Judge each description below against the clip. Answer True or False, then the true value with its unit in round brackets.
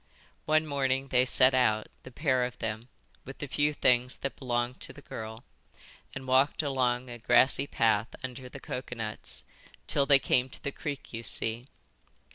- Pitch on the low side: True (130 Hz)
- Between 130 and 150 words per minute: False (170 wpm)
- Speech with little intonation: True (2.2 semitones)